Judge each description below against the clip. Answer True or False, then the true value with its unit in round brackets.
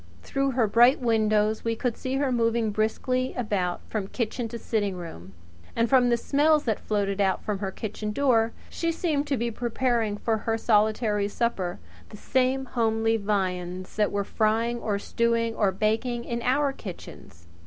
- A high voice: True (225 Hz)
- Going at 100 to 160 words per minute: False (170 wpm)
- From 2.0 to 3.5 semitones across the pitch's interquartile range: True (2.8 semitones)